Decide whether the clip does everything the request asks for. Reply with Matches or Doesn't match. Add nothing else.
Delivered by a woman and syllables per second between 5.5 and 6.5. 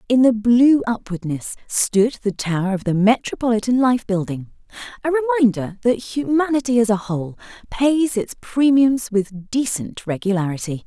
Doesn't match